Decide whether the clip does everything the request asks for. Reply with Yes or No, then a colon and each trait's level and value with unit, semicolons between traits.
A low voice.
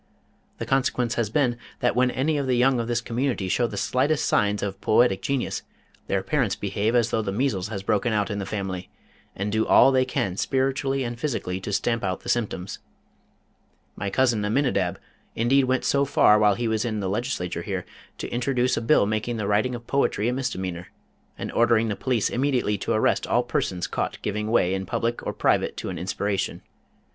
Yes: low, 115 Hz